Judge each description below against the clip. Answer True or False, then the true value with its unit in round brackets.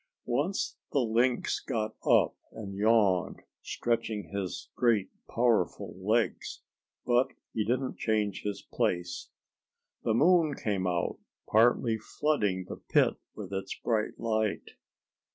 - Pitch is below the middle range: True (110 Hz)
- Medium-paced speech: False (115 wpm)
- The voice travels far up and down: False (3.1 semitones)